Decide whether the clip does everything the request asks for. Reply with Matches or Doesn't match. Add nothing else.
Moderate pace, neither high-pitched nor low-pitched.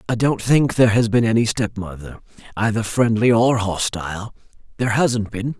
Doesn't match